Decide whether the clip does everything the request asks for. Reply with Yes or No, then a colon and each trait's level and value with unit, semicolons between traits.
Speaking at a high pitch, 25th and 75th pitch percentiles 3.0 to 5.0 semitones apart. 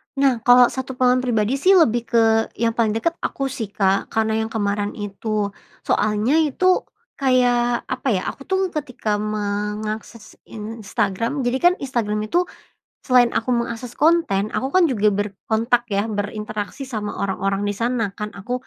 Yes: high, 230 Hz; average, 3.6 semitones